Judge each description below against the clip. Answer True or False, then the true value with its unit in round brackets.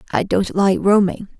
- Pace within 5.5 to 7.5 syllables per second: False (4.6 syllables/s)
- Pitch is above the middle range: True (195 Hz)